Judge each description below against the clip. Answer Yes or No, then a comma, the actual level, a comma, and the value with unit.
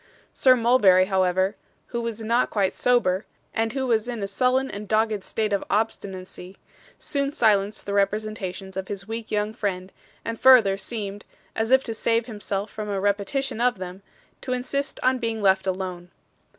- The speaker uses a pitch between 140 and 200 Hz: No, high, 210 Hz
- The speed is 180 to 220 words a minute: No, average, 170 wpm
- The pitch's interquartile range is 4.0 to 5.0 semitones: No, average, 3.3 semitones